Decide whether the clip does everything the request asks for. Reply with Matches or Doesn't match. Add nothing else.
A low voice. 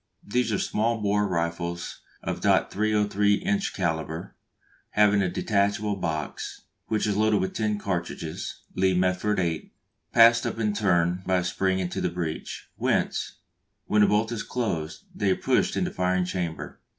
Matches